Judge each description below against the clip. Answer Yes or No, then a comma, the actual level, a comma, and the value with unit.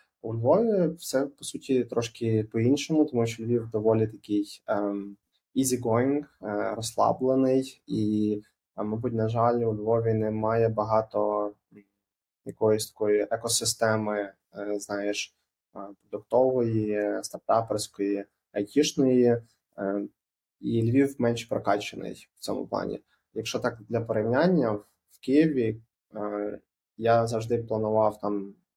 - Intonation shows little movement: Yes, narrow, 2.2 semitones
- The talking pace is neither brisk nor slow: No, slow, 95 wpm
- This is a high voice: No, low, 110 Hz